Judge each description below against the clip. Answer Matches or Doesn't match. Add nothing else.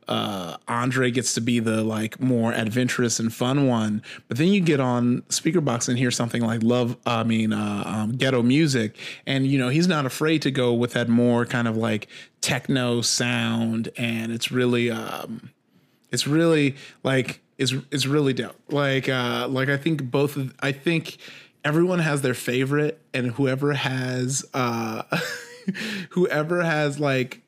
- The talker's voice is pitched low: Matches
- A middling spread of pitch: Matches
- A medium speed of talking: Matches